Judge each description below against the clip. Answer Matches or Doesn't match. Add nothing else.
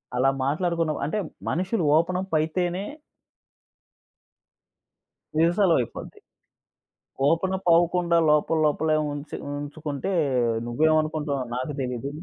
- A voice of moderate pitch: Matches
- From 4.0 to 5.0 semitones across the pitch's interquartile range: Doesn't match